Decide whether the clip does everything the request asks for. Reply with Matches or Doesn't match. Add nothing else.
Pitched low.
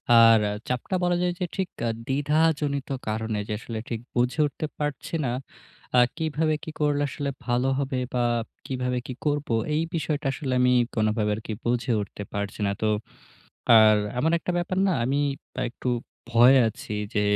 Matches